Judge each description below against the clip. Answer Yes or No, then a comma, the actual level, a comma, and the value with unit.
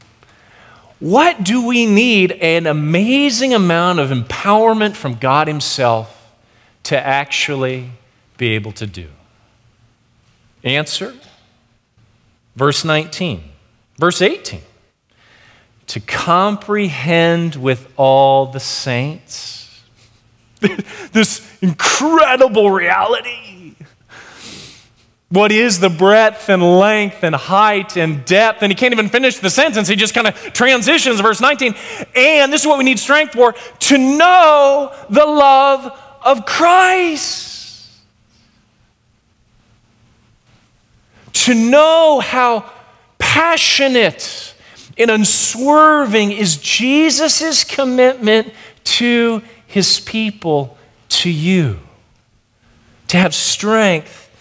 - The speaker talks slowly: Yes, slow, 95 wpm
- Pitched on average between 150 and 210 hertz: Yes, medium, 185 Hz